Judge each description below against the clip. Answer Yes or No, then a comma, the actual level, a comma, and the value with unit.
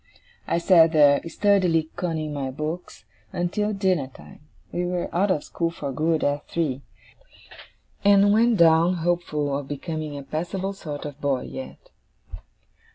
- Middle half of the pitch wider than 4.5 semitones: No, average, 3.8 semitones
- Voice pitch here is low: No, medium, 165 Hz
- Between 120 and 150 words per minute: Yes, average, 145 wpm